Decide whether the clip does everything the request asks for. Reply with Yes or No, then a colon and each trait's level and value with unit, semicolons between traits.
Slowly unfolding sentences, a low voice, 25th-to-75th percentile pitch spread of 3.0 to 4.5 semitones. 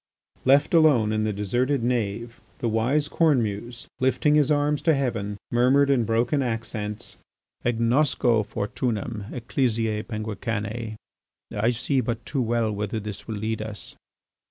Yes: slow, 130 wpm; low, 115 Hz; average, 3.3 semitones